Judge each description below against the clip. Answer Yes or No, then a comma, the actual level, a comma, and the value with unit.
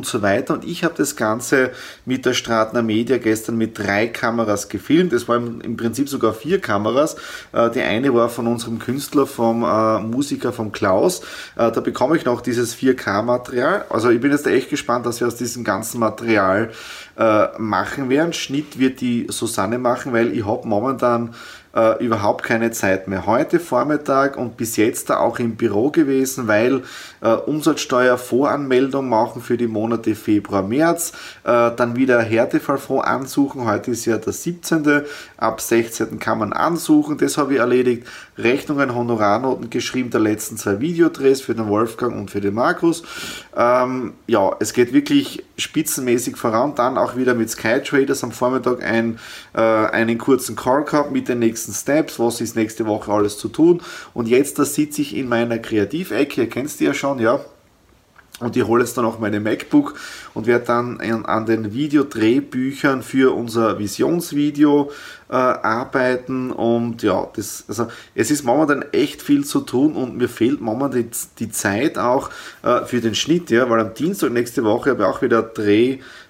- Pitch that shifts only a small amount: No, average, 3.7 semitones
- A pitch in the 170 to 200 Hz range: No, low, 120 Hz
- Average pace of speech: Yes, average, 170 wpm